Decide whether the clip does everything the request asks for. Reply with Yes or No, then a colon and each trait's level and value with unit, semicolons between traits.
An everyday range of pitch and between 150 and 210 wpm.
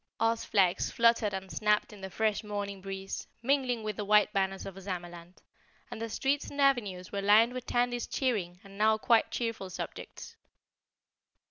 Yes: average, 3.2 semitones; average, 165 wpm